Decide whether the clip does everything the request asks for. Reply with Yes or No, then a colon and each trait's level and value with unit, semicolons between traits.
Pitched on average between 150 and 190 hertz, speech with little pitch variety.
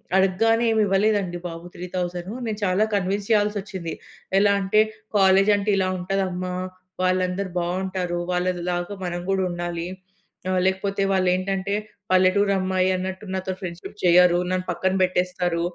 Yes: medium, 185 Hz; narrow, 1.5 semitones